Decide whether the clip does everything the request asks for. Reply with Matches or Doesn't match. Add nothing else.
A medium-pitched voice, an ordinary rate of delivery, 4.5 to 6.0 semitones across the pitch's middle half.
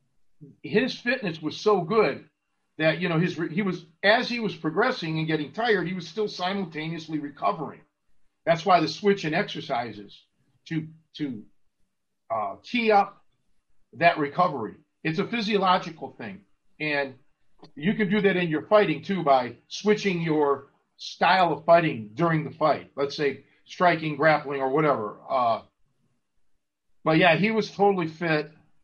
Matches